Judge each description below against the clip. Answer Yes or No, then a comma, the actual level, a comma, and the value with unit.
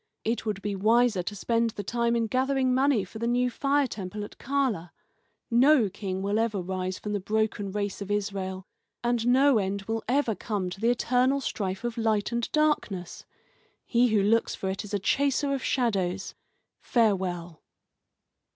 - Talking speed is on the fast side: No, average, 175 wpm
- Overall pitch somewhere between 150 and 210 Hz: No, high, 220 Hz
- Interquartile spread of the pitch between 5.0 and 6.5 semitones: No, average, 3.9 semitones